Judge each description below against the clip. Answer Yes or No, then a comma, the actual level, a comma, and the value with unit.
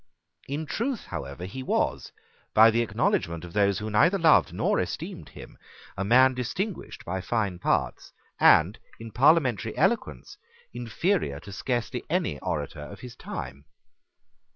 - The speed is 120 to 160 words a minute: Yes, average, 140 wpm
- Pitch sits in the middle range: No, low, 115 Hz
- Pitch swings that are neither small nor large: No, wide, 6.2 semitones